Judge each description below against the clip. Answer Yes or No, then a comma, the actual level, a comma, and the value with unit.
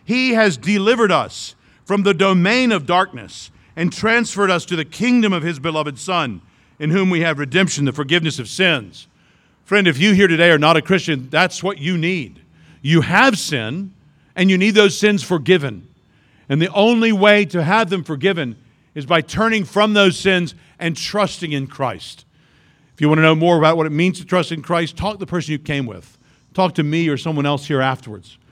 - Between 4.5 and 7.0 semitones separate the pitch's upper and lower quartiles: Yes, average, 4.9 semitones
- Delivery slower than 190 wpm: No, fast, 205 wpm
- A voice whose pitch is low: No, medium, 170 Hz